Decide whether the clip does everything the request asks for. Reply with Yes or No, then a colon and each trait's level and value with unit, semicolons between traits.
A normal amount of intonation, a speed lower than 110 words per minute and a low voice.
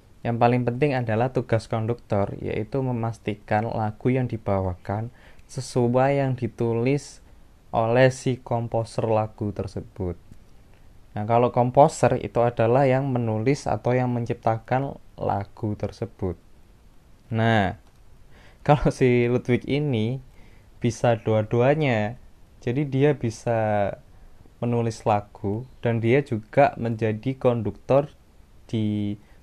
Yes: average, 3.2 semitones; average, 100 wpm; low, 115 Hz